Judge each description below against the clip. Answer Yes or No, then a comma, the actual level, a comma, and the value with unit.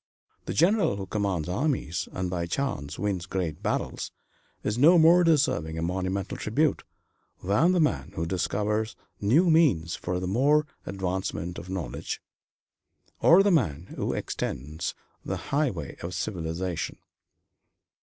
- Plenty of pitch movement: Yes, wide, 9.0 semitones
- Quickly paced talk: No, slow, 135 wpm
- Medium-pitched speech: No, very low, 95 Hz